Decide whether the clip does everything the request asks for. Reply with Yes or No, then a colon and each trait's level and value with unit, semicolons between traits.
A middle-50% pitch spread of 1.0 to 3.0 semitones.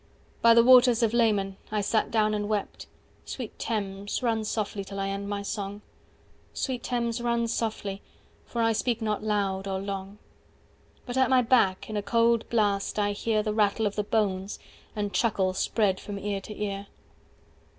Yes: narrow, 2.5 semitones